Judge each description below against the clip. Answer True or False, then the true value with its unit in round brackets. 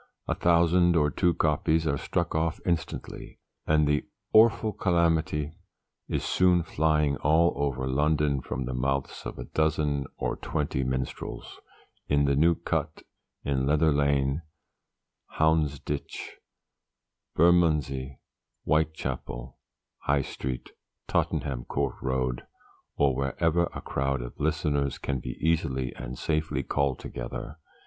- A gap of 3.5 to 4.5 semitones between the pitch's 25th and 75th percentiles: False (3.0 semitones)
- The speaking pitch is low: True (75 Hz)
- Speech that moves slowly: True (120 wpm)